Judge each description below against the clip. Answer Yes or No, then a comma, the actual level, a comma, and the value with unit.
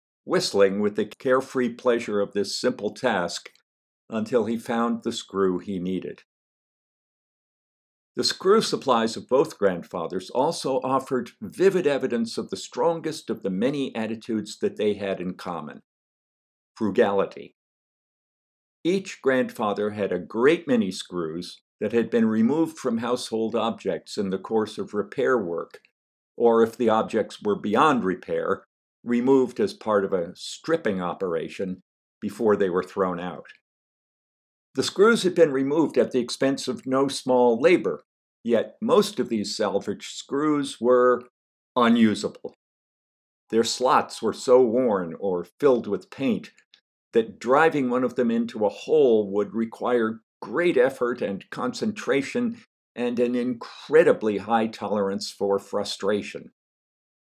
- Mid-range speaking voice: No, low, 120 Hz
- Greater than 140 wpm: No, slow, 135 wpm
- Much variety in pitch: No, average, 4.1 semitones